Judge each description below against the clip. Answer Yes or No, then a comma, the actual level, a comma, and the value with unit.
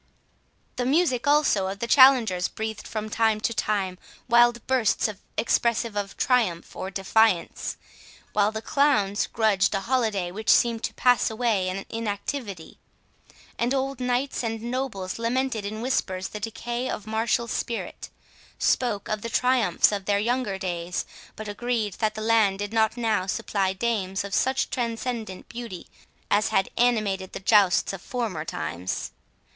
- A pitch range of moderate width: Yes, average, 3.5 semitones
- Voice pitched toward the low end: No, high, 220 Hz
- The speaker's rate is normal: Yes, average, 150 wpm